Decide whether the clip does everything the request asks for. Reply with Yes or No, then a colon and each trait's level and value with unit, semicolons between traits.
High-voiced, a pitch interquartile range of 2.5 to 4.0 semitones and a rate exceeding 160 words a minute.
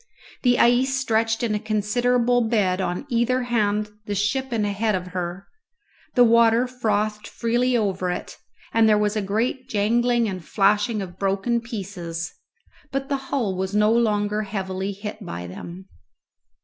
No: high, 215 Hz; average, 3.4 semitones; average, 155 wpm